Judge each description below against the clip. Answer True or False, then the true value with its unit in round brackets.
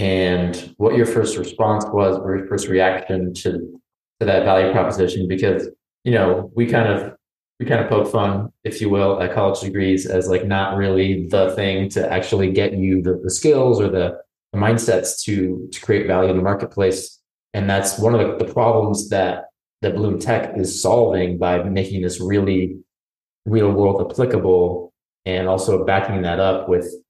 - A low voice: True (95 Hz)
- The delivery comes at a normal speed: True (180 wpm)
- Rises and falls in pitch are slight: True (1.4 semitones)